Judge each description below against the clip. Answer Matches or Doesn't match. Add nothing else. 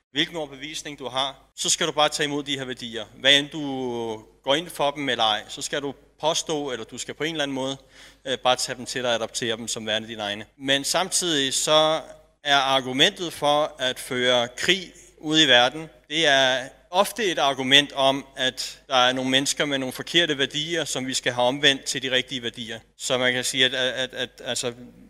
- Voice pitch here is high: Doesn't match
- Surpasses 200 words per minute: Matches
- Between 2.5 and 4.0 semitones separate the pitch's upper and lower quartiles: Matches